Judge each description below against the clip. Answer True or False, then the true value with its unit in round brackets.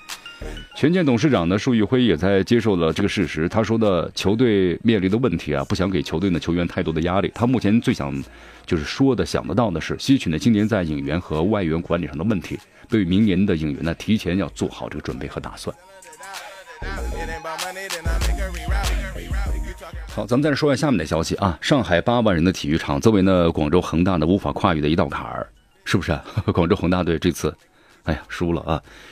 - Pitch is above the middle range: False (90 Hz)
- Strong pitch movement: False (4.9 semitones)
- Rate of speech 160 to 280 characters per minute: False (300 characters per minute)